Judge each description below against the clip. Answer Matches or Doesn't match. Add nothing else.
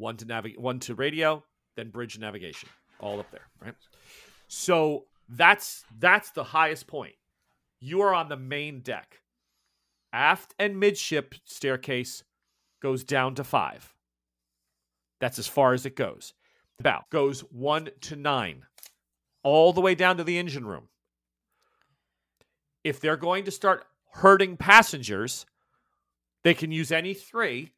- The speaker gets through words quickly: Doesn't match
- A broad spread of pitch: Matches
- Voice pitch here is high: Doesn't match